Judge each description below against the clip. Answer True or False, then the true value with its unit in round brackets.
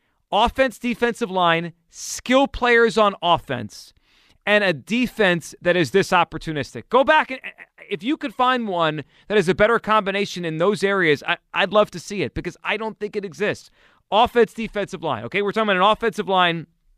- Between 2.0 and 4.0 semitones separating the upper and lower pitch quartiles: False (4.6 semitones)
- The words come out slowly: False (185 wpm)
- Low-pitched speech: False (200 Hz)